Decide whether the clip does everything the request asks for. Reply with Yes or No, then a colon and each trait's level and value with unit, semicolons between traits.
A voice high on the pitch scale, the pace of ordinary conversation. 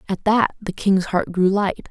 No: high, 195 Hz; fast, 220 wpm